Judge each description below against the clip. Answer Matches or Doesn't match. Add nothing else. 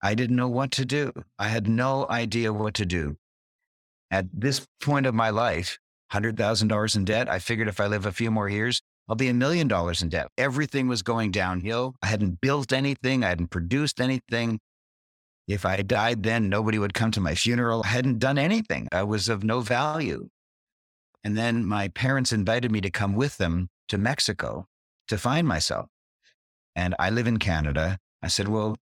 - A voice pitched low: Matches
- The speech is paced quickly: Doesn't match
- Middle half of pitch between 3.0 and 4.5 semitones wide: Matches